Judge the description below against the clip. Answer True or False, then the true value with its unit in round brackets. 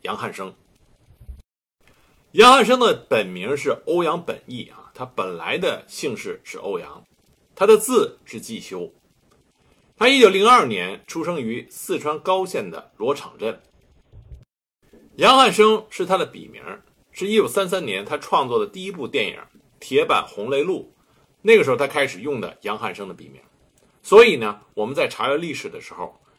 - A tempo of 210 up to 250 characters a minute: True (235 characters per minute)